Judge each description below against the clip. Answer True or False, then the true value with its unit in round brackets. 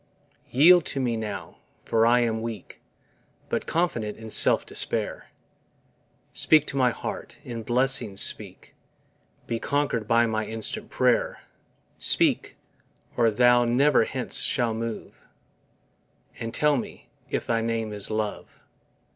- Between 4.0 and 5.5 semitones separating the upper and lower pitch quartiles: False (2.4 semitones)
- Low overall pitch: True (115 Hz)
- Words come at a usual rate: False (130 wpm)